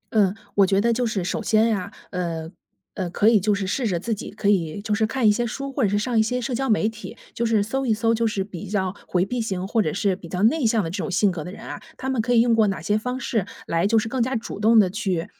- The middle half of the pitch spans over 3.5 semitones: No, average, 3.2 semitones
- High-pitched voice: Yes, high, 215 Hz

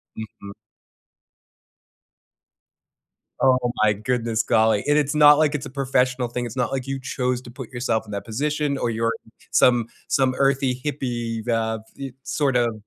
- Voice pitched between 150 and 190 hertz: No, low, 125 Hz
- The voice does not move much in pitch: No, average, 3.0 semitones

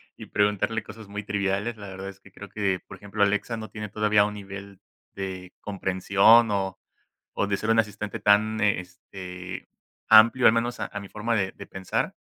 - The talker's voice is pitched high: No, low, 100 Hz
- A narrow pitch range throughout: Yes, narrow, 1.7 semitones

